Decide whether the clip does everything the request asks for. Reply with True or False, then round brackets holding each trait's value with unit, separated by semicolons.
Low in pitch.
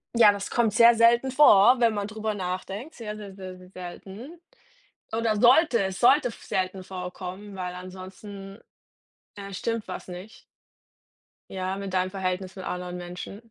False (195 Hz)